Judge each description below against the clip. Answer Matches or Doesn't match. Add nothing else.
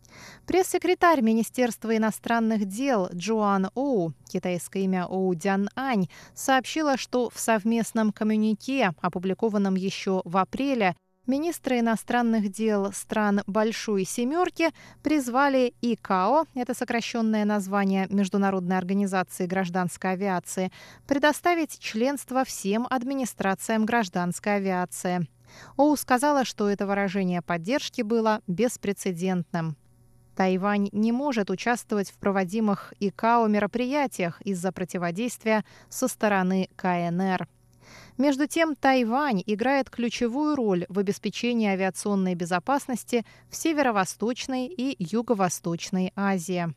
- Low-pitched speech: Doesn't match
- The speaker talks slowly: Matches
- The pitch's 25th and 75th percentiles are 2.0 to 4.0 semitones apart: Doesn't match